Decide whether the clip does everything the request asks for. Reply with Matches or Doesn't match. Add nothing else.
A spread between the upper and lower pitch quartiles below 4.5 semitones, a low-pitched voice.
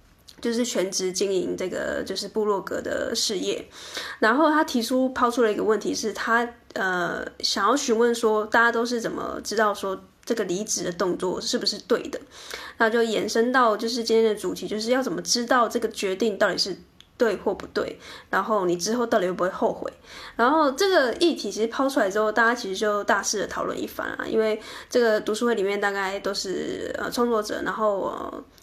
Doesn't match